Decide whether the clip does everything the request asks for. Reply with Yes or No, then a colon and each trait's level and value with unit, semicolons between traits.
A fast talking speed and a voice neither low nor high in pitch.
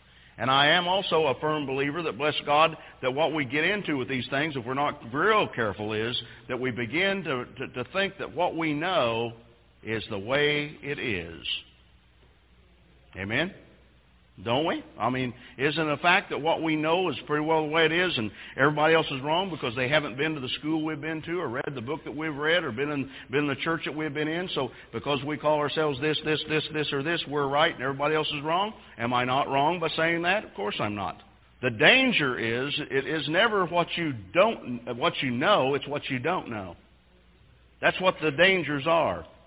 Yes: fast, 220 wpm; medium, 145 Hz